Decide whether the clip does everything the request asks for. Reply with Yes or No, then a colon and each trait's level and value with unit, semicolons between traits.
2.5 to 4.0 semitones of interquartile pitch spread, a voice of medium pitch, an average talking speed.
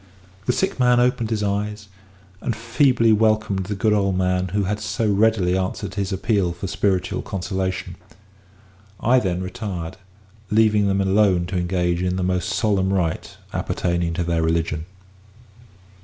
No: average, 2.9 semitones; very low, 95 Hz; average, 150 wpm